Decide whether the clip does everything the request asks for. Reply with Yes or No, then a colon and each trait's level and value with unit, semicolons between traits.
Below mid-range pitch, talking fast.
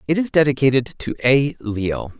No: low, 130 Hz; average, 165 wpm